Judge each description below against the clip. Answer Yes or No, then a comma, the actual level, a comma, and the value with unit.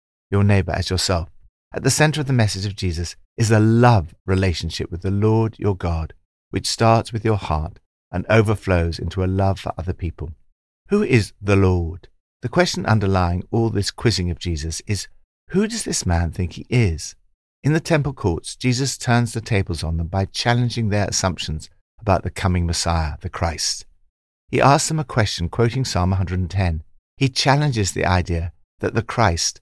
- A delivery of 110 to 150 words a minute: No, average, 180 wpm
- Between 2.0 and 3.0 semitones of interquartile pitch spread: No, average, 5.1 semitones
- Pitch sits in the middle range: No, very low, 95 Hz